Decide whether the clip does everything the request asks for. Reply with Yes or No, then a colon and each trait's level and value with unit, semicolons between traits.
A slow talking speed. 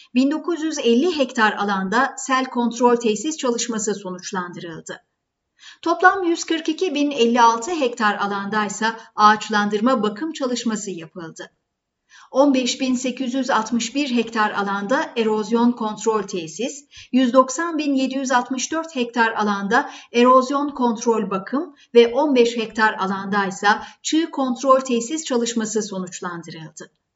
Yes: slow, 85 wpm